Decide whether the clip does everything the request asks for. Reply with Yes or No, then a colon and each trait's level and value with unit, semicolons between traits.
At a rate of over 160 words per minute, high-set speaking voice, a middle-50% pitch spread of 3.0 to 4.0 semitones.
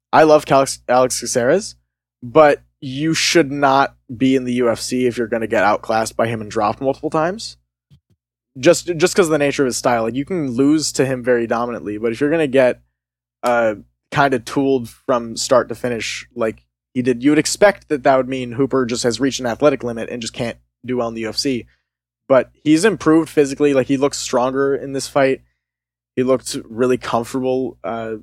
No: fast, 205 wpm; low, 125 Hz; average, 3.6 semitones